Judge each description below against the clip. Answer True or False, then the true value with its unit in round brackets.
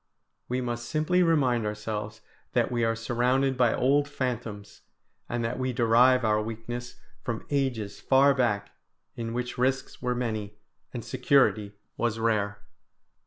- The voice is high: False (120 Hz)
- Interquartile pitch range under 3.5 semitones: True (2.6 semitones)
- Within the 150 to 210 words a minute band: False (140 wpm)